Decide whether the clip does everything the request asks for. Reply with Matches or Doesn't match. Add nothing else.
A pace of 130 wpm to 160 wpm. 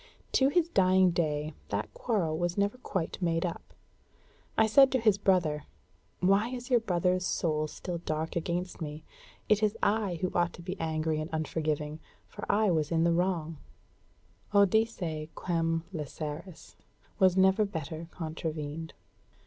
Matches